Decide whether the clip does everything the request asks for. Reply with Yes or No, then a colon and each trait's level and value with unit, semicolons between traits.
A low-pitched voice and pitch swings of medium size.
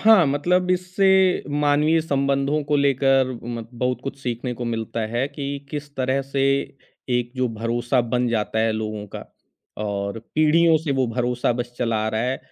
Yes: low, 130 Hz; average, 3.5 semitones